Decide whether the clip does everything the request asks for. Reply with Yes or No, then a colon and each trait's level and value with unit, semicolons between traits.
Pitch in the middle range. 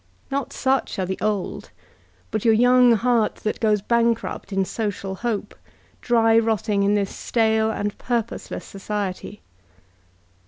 No: high, 220 Hz